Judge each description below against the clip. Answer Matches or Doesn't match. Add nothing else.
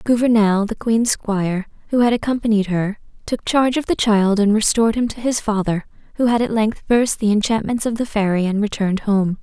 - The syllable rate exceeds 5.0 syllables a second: Matches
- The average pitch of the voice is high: Matches